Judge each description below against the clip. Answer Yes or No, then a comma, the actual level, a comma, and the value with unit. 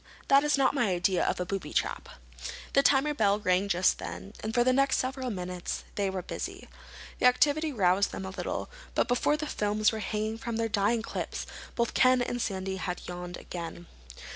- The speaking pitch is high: Yes, high, 215 Hz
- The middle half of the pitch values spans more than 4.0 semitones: Yes, average, 5.1 semitones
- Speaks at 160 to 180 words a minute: No, average, 195 wpm